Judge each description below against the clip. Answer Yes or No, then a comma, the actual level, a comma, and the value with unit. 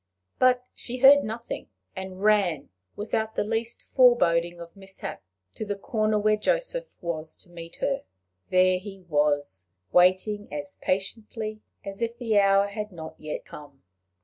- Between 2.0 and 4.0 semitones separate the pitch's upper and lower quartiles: No, average, 4.4 semitones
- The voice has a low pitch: No, high, 200 Hz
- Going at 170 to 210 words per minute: No, average, 150 wpm